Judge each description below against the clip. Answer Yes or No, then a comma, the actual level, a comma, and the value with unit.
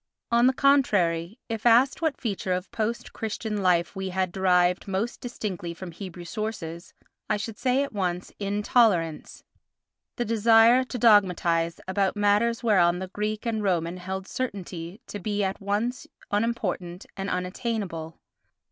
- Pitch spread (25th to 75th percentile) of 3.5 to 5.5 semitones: Yes, average, 4.0 semitones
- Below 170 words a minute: Yes, average, 140 wpm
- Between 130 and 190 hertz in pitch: No, high, 200 Hz